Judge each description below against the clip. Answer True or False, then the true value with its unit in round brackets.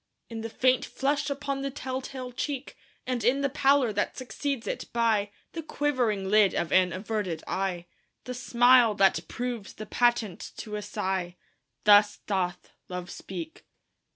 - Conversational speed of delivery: True (155 wpm)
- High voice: True (225 Hz)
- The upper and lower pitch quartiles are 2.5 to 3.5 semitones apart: False (4.8 semitones)